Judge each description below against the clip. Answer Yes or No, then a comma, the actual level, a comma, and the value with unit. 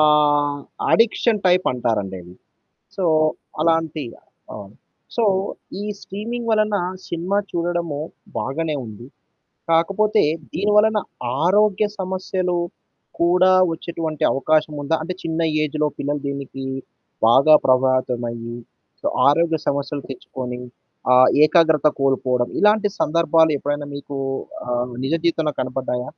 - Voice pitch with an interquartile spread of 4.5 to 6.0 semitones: Yes, average, 5.2 semitones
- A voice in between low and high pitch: Yes, medium, 155 Hz